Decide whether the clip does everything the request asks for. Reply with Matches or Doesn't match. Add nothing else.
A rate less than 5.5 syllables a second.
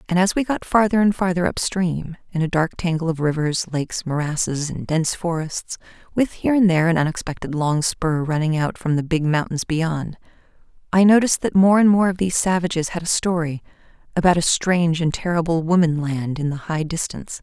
Doesn't match